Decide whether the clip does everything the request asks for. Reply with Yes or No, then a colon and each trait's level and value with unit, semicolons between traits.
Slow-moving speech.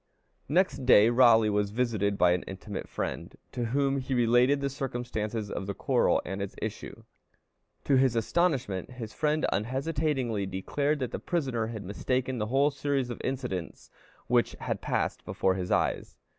No: average, 160 wpm